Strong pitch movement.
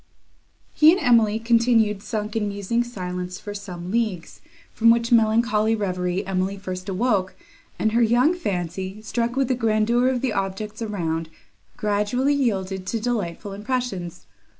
No: average, 3.7 semitones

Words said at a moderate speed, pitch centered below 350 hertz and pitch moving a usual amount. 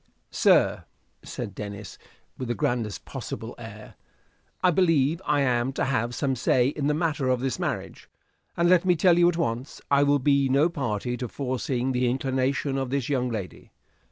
Yes: average, 180 wpm; low, 135 Hz; average, 3.0 semitones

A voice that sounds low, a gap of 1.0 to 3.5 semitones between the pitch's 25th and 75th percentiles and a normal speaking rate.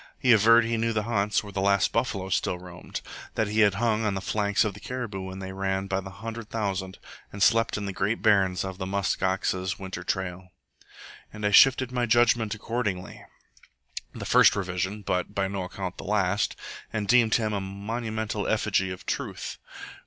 Yes: low, 100 Hz; narrow, 2.6 semitones; average, 190 wpm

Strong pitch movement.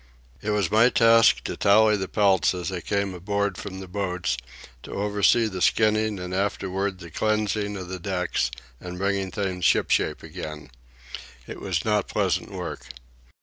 No: narrow, 2.4 semitones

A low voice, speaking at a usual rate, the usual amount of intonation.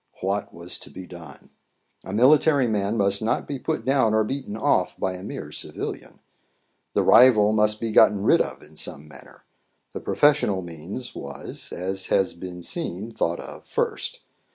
Yes: low, 105 Hz; average, 170 wpm; average, 4.3 semitones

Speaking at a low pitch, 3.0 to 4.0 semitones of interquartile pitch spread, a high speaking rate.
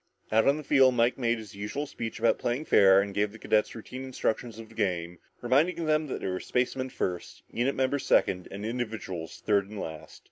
No: low, 115 Hz; average, 4.5 semitones; fast, 215 wpm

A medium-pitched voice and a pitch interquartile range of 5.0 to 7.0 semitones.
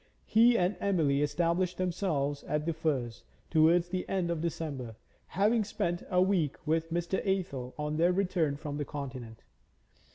No: medium, 165 Hz; average, 3.8 semitones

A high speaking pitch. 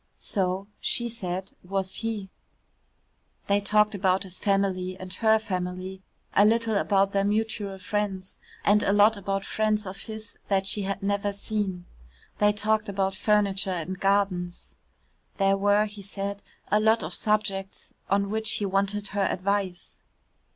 Yes: high, 200 Hz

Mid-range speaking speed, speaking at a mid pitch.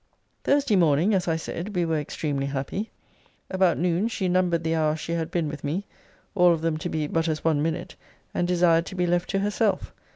No: fast, 215 wpm; medium, 170 Hz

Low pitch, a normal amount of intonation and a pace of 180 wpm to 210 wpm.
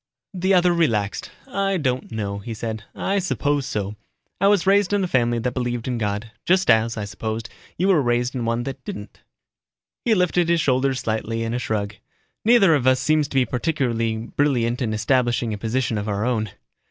No: low, 125 Hz; wide, 5.8 semitones; average, 195 wpm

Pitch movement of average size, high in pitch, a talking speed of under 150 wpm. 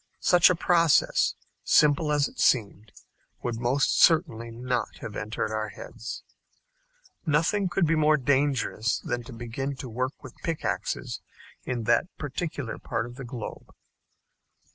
No: average, 4.7 semitones; low, 130 Hz; average, 140 wpm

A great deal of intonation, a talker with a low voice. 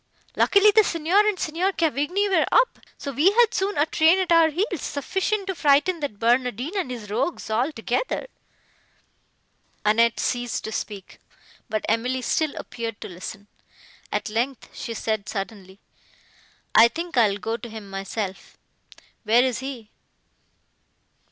No: wide, 7.7 semitones; very high, 255 Hz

